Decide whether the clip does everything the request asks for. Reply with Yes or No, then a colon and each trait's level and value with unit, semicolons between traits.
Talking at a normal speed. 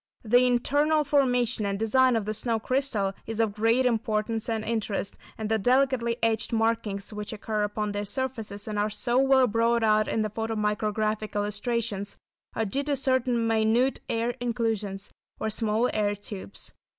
Yes: average, 165 wpm